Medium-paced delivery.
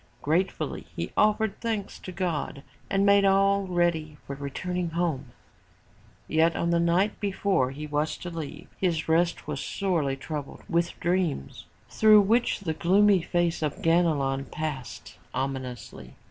Yes: average, 160 wpm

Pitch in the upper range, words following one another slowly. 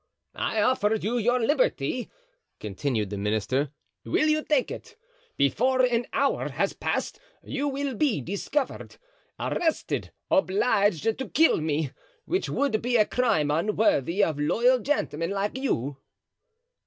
Yes: high, 220 Hz; slow, 130 wpm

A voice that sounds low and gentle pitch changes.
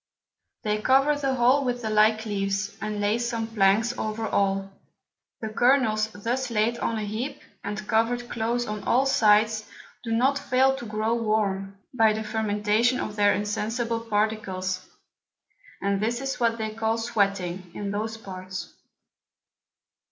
No: high, 220 Hz; narrow, 2.3 semitones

